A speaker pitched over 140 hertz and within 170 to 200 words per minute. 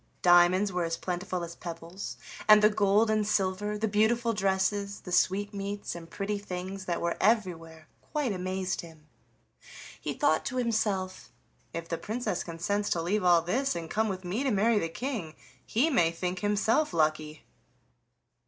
No: high, 190 Hz; average, 160 wpm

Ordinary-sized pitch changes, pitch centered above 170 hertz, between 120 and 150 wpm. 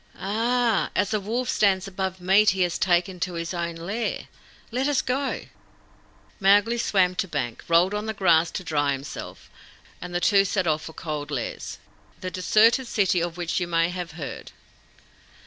No: average, 3.6 semitones; medium, 185 Hz; average, 175 wpm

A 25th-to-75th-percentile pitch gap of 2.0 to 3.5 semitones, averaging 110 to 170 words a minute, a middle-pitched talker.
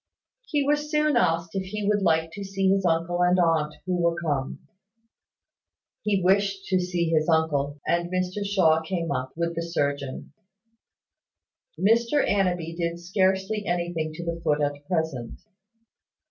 Yes: average, 3.2 semitones; average, 150 wpm; medium, 175 Hz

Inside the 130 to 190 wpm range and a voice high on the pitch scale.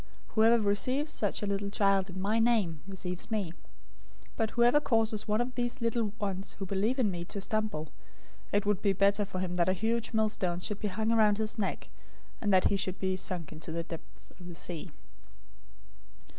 No: average, 200 wpm; high, 205 Hz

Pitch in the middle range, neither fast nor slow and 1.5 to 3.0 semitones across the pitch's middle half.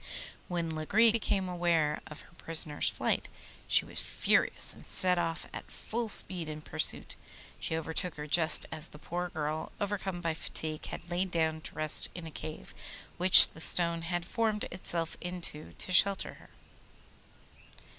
Yes: medium, 170 Hz; average, 160 wpm; narrow, 2.5 semitones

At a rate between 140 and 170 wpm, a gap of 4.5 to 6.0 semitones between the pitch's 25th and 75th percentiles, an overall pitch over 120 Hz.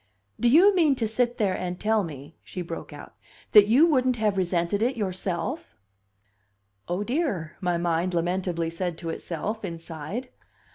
Yes: average, 155 wpm; wide, 5.5 semitones; high, 190 Hz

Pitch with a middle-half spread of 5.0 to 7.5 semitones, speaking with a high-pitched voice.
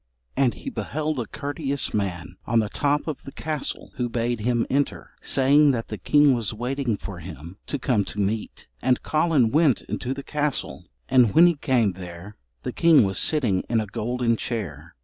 No: wide, 5.4 semitones; low, 120 Hz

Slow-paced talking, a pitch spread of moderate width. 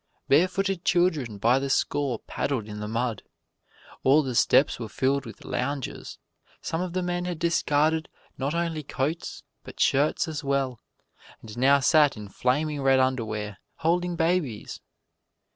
No: average, 145 wpm; average, 4.6 semitones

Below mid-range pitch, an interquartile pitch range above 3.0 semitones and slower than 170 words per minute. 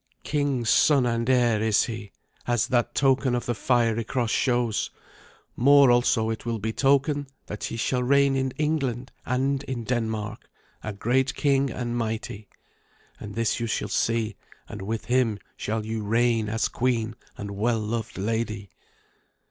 No: low, 120 Hz; average, 2.7 semitones; average, 155 wpm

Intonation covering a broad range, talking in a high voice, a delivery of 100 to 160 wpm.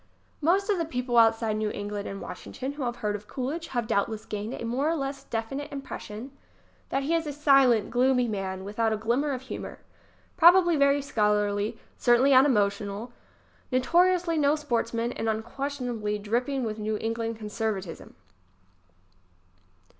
No: average, 4.6 semitones; high, 240 Hz; average, 155 wpm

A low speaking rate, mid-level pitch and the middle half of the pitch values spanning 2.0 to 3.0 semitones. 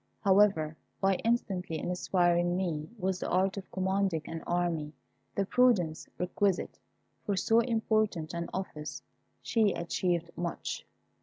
Yes: slow, 130 wpm; medium, 180 Hz; average, 2.7 semitones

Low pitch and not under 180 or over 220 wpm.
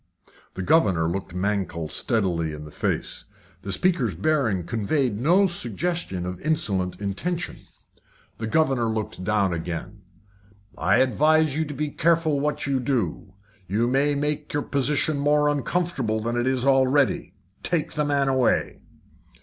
No: low, 130 Hz; average, 140 wpm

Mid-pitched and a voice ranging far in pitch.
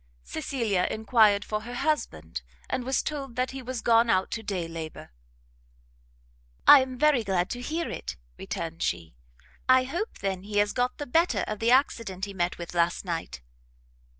No: high, 220 Hz; wide, 5.8 semitones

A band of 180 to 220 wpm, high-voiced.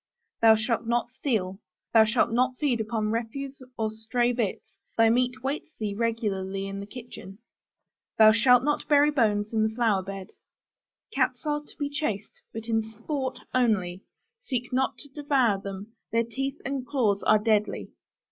No: average, 165 wpm; high, 230 Hz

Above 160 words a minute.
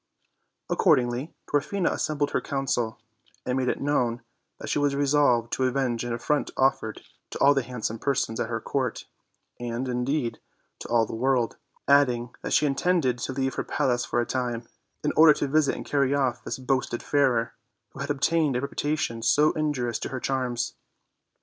Yes: average, 180 wpm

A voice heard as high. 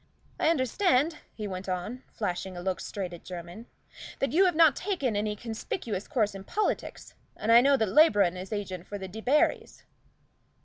Yes: high, 215 Hz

